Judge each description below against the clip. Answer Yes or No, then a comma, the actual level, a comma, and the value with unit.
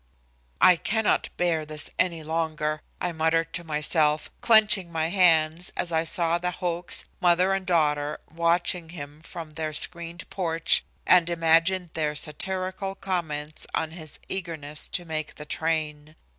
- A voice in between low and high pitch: Yes, medium, 165 Hz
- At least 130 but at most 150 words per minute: Yes, average, 145 wpm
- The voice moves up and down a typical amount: No, narrow, 2.3 semitones